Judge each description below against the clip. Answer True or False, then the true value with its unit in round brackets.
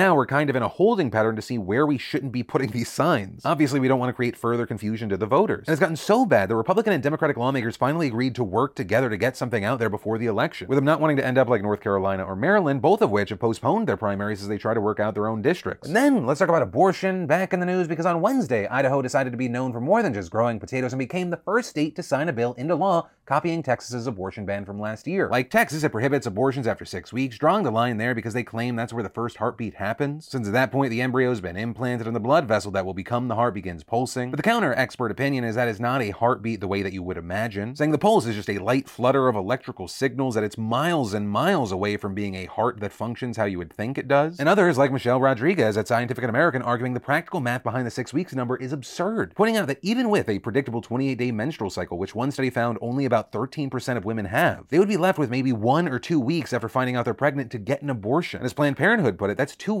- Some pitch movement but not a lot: True (4.4 semitones)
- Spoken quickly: True (280 wpm)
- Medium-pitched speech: False (125 Hz)